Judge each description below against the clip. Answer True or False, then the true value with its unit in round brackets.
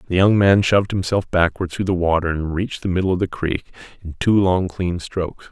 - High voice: False (90 Hz)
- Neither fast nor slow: False (230 wpm)